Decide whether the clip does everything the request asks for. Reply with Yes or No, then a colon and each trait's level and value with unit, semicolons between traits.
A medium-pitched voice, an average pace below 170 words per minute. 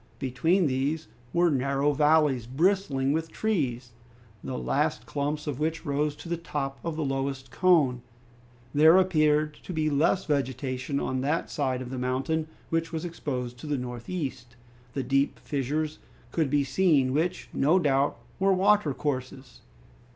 Yes: medium, 145 Hz; average, 150 wpm